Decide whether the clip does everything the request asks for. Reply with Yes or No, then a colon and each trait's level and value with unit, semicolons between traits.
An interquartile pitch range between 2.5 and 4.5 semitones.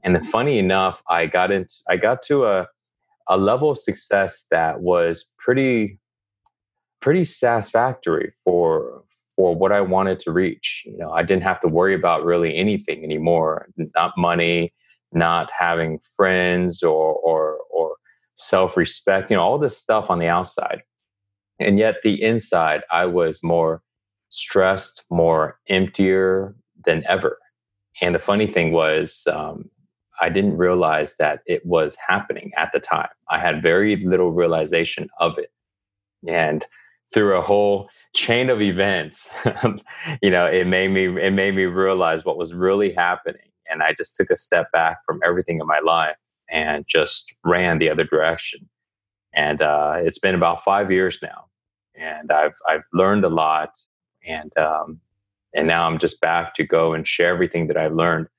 Yes: average, 3.2 semitones